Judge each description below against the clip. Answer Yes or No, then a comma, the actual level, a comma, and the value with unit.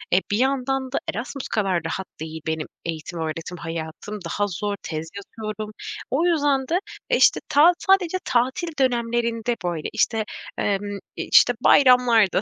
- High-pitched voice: Yes, high, 220 Hz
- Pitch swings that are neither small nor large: No, wide, 7.1 semitones